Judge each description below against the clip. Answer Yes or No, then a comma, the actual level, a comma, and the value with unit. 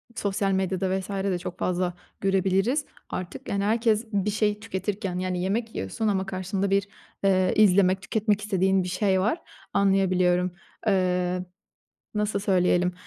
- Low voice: No, high, 195 Hz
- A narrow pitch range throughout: Yes, narrow, 1.9 semitones